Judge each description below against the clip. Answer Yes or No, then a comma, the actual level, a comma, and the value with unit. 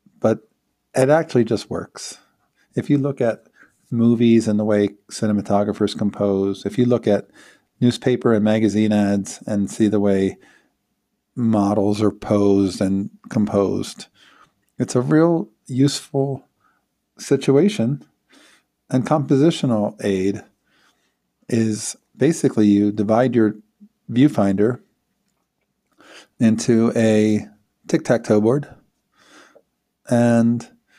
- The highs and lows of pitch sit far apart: No, average, 3.2 semitones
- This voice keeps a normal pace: No, slow, 100 wpm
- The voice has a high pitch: No, low, 110 Hz